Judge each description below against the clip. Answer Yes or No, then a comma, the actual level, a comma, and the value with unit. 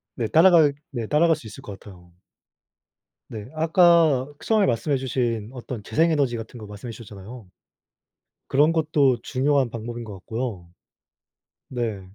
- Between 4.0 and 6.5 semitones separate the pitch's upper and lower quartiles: Yes, average, 5.3 semitones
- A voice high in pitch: No, low, 125 Hz